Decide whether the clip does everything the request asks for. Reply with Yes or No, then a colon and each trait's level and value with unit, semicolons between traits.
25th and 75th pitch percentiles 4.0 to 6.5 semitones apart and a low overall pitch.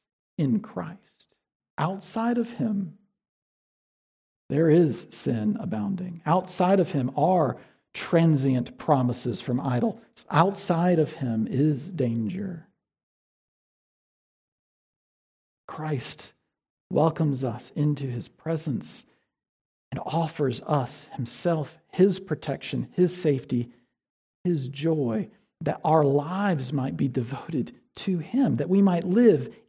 No: wide, 5.5 semitones; medium, 155 Hz